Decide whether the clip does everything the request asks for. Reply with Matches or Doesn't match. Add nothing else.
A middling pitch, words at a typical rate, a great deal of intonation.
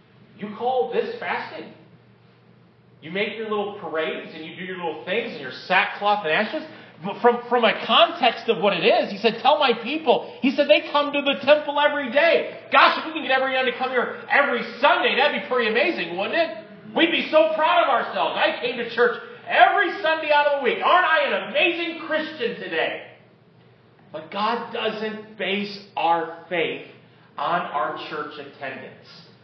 Doesn't match